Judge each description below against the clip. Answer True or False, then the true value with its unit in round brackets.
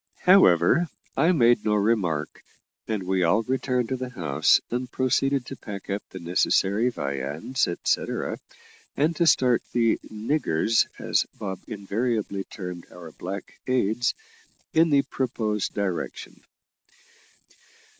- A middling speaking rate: False (125 wpm)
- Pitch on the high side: False (110 Hz)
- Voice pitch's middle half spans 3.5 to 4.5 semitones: False (5.2 semitones)